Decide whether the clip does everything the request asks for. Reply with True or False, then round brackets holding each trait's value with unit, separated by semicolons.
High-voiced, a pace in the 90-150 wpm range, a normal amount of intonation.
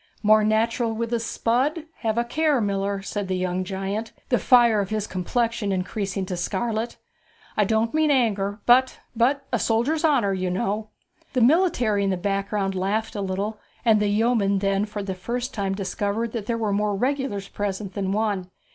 False (210 Hz; 180 wpm; 3.2 semitones)